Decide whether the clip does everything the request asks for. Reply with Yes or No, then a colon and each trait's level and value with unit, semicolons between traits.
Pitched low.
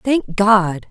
No: high, 200 Hz